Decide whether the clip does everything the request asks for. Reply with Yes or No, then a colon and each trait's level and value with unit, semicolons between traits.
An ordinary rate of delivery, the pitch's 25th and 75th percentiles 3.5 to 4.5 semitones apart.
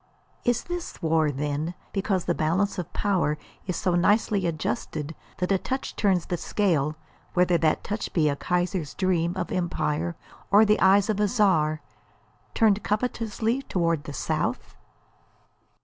Yes: average, 150 wpm; average, 4.2 semitones